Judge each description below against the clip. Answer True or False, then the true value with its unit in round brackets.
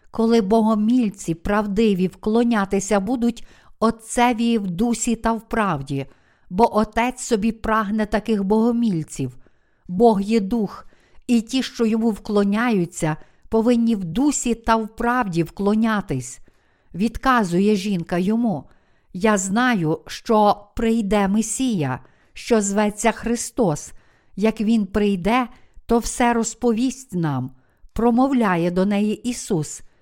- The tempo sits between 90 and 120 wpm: True (110 wpm)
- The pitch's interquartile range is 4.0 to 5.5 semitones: False (3.1 semitones)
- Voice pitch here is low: False (220 Hz)